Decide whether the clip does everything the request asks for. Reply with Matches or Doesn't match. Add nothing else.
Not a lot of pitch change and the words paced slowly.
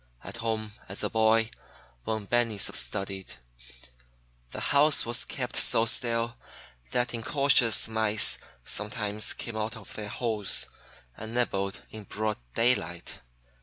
Matches